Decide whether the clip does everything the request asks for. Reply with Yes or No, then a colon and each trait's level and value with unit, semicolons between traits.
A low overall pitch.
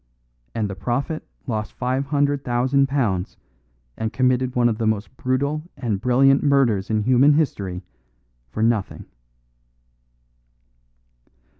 Yes: low, 125 Hz